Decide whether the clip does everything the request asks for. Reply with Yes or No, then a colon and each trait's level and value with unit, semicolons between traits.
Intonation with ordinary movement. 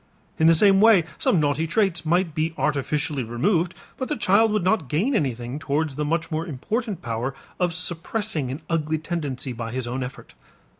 Yes: average, 4.9 semitones